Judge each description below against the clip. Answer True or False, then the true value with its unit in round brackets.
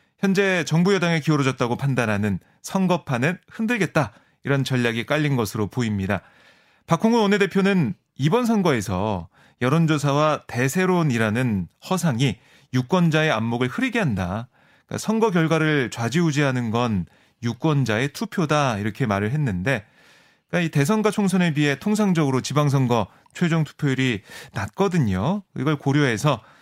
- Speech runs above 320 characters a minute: True (335 characters per minute)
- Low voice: False (145 Hz)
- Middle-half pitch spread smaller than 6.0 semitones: False (6.6 semitones)